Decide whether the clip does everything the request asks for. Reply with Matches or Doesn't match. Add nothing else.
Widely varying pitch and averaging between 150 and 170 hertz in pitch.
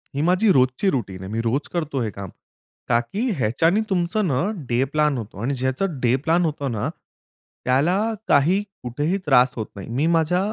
Doesn't match